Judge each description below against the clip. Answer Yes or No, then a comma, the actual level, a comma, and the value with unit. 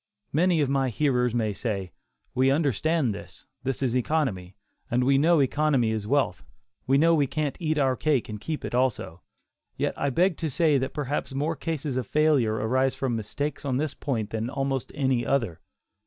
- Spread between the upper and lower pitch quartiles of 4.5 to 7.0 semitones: No, average, 3.9 semitones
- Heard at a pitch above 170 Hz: No, low, 135 Hz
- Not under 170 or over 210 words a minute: Yes, average, 185 wpm